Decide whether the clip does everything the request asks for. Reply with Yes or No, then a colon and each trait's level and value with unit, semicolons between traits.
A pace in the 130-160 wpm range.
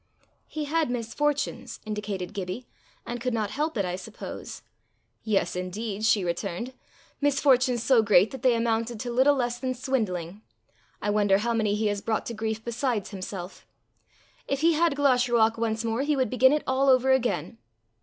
No: average, 175 wpm